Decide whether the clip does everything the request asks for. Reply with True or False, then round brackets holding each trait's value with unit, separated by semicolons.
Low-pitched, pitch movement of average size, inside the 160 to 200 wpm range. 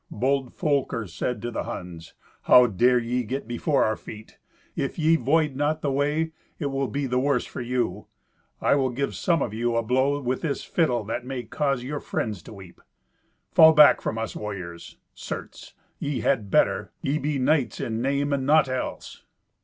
True (130 Hz; 3.6 semitones; 185 wpm)